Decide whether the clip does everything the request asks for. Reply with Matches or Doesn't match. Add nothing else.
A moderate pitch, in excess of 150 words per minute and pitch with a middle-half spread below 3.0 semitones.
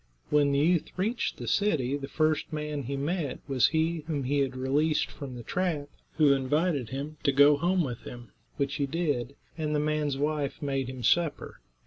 Matches